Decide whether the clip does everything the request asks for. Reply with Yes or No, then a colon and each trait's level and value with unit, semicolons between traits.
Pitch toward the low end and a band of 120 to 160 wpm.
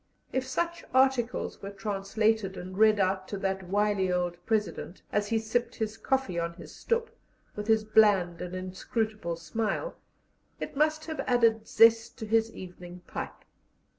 No: high, 215 Hz; average, 155 wpm